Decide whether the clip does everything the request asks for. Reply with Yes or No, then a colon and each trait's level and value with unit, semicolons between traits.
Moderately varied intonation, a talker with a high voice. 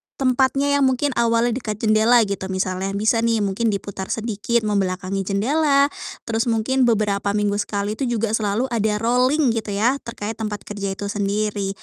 Yes: average, 3.0 semitones; high, 215 Hz